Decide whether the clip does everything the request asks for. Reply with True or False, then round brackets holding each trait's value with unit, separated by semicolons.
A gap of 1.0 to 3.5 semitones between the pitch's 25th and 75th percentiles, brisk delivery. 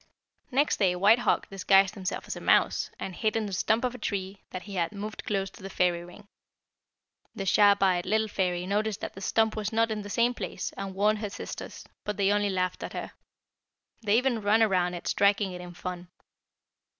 True (2.6 semitones; 210 wpm)